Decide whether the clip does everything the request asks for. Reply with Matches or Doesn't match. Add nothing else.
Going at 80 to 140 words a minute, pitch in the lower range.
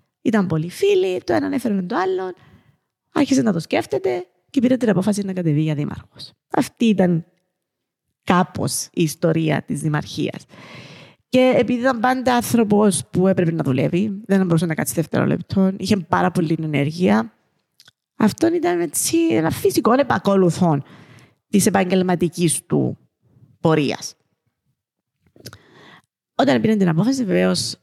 Doesn't match